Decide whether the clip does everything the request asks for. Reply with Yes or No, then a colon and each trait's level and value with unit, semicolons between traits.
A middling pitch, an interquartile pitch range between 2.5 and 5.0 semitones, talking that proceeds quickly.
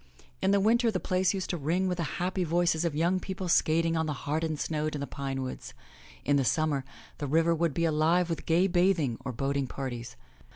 Yes: medium, 165 Hz; average, 3.9 semitones; fast, 215 wpm